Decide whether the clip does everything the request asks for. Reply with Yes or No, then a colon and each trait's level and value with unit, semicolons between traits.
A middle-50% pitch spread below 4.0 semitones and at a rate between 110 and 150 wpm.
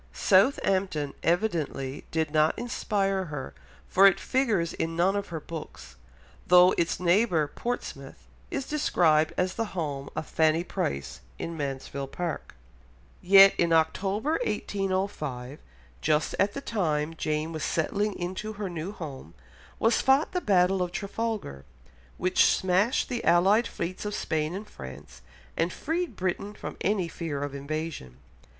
No: average, 4.7 semitones; average, 140 wpm